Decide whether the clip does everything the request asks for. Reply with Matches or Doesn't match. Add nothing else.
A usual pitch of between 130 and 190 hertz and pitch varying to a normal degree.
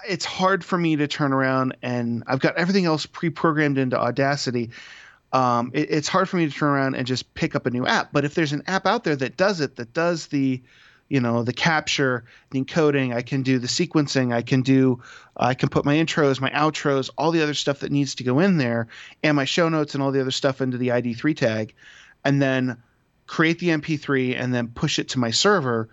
Matches